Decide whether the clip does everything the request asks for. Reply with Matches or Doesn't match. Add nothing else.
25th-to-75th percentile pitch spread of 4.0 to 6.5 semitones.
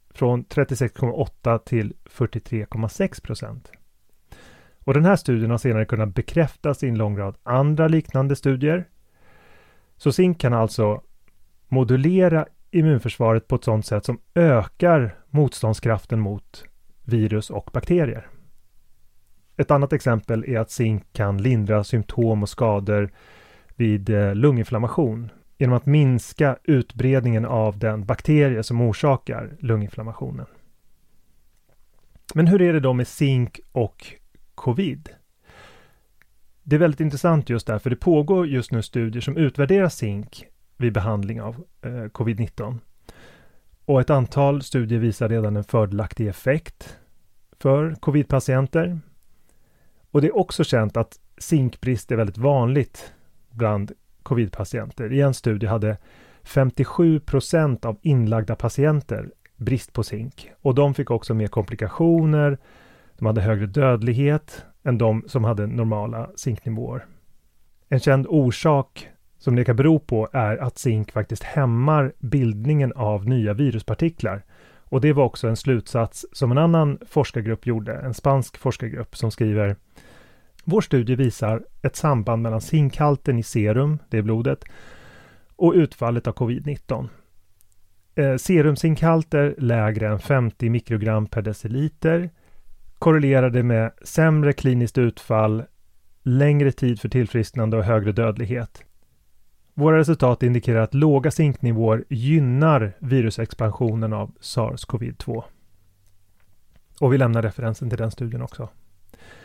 Matches